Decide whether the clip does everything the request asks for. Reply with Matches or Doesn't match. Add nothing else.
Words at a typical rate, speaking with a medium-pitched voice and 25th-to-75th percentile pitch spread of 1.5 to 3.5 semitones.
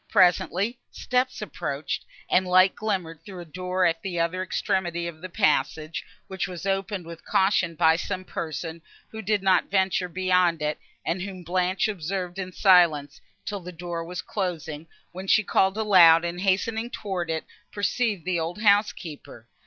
Matches